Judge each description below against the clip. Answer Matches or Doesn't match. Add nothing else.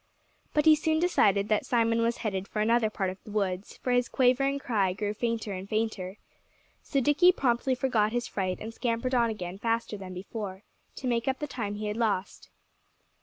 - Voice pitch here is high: Matches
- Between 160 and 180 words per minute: Doesn't match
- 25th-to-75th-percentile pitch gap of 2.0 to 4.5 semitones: Matches